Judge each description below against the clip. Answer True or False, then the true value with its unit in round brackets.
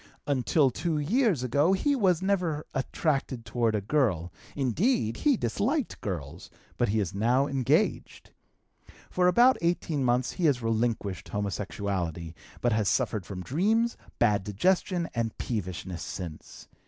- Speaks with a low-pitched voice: True (125 Hz)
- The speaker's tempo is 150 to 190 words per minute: False (135 wpm)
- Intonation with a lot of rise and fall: True (9.0 semitones)